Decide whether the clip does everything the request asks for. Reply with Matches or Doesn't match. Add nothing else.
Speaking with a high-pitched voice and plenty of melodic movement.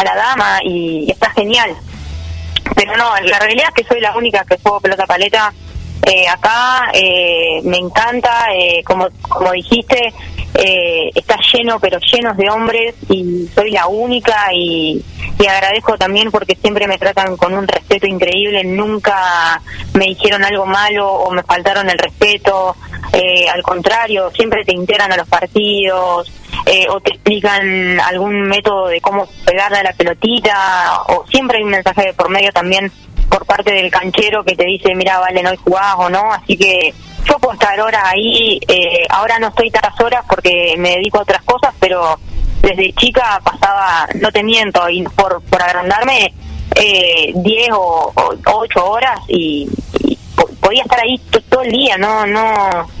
Doesn't match